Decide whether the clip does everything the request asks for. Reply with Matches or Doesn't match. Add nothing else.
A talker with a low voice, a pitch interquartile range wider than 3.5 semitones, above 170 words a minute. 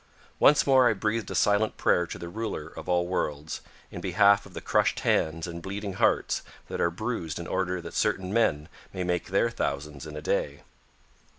Matches